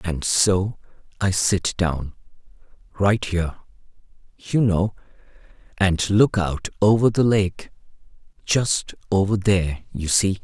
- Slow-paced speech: Yes, slow, 100 wpm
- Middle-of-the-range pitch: No, very low, 95 Hz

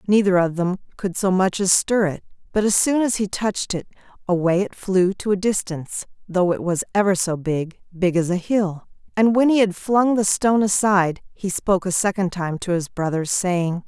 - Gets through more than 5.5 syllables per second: No, 5.1 syllables/s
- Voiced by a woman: Yes, female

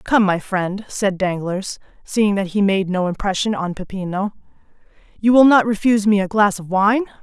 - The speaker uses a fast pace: No, average, 185 wpm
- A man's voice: No, female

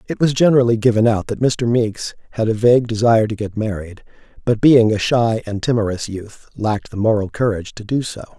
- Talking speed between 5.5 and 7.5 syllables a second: Yes, 5.8 syllables/s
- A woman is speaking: No, male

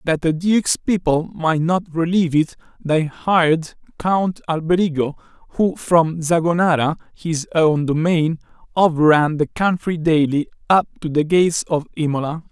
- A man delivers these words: Yes, male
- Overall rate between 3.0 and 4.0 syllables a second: No, 4.5 syllables/s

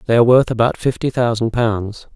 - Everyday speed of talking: Yes, average, 195 wpm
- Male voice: Yes, male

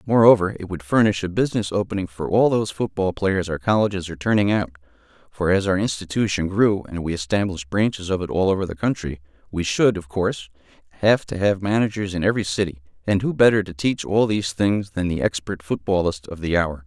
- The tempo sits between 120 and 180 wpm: No, fast, 205 wpm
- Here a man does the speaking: Yes, male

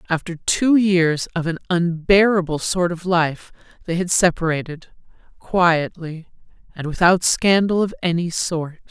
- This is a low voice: No, medium, 175 Hz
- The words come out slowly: Yes, slow, 120 wpm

